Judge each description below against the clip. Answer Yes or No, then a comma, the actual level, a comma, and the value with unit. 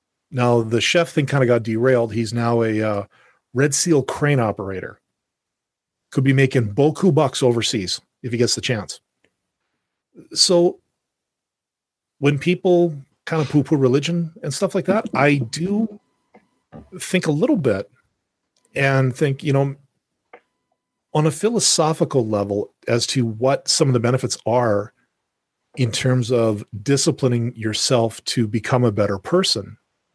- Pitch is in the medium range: No, low, 130 Hz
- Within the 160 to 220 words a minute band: No, average, 140 wpm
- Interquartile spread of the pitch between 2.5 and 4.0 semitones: No, average, 5.0 semitones